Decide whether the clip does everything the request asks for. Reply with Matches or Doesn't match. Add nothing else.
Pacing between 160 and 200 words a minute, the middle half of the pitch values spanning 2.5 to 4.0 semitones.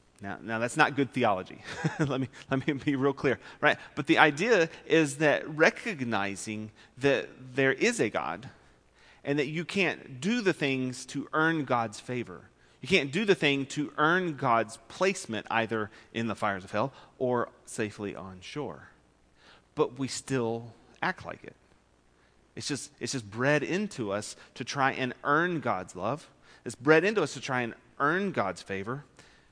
Doesn't match